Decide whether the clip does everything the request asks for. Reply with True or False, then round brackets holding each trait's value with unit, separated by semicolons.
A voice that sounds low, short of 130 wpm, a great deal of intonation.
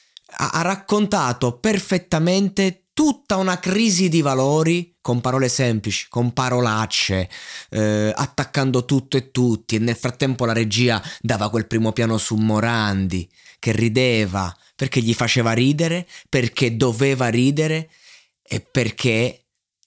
True (125 Hz; 120 wpm; 5.7 semitones)